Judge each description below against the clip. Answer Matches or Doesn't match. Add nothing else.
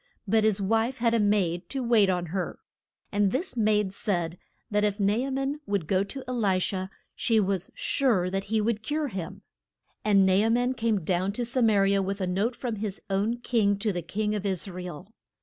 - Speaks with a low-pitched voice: Doesn't match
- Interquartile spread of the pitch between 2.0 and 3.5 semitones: Matches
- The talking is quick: Matches